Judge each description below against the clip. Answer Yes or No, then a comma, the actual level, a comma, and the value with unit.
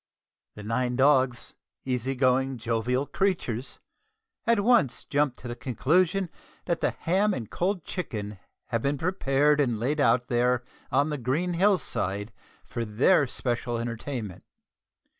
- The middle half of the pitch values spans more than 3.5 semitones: Yes, average, 4.7 semitones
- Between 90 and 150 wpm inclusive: Yes, average, 140 wpm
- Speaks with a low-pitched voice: Yes, low, 130 Hz